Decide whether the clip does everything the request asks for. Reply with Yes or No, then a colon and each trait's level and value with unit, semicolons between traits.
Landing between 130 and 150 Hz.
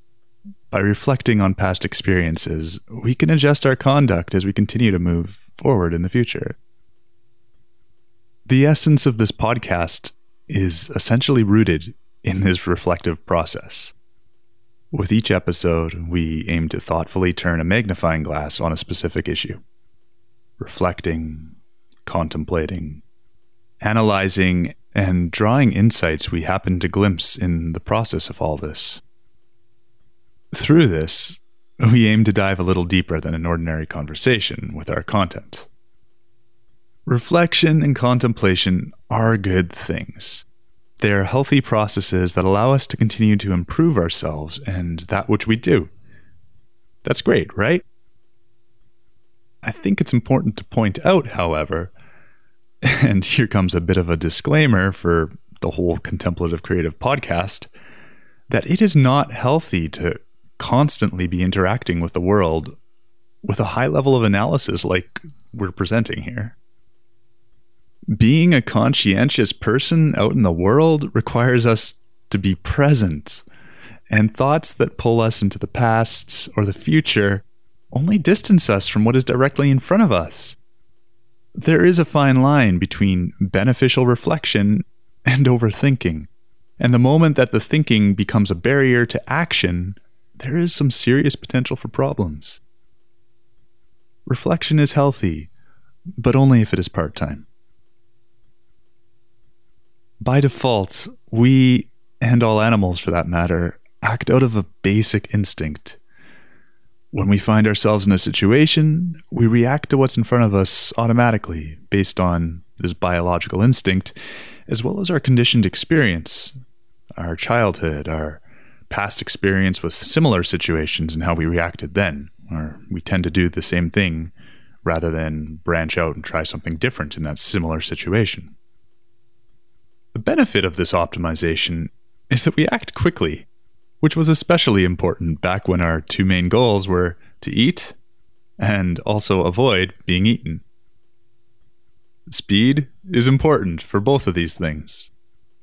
No: low, 110 Hz